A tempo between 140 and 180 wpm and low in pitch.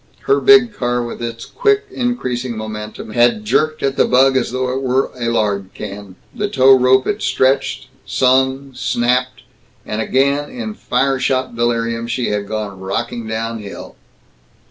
Yes: average, 160 wpm; low, 125 Hz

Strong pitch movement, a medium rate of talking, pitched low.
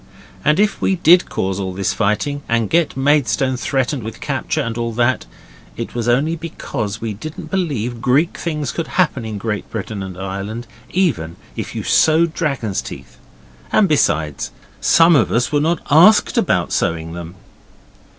Yes: wide, 6.8 semitones; average, 165 wpm; low, 125 Hz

